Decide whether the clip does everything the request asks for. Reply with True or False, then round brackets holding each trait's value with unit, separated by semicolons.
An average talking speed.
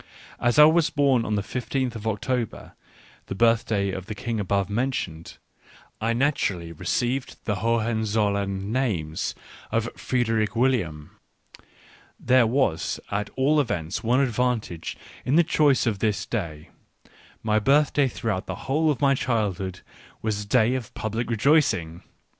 True (145 wpm)